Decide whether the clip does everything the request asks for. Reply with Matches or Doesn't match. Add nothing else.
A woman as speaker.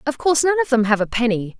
Matches